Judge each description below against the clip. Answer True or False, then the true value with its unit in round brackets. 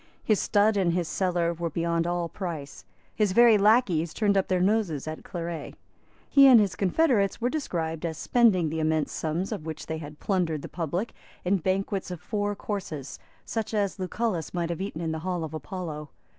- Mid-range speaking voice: True (180 Hz)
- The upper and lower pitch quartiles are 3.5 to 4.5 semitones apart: True (4.0 semitones)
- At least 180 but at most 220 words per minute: True (190 wpm)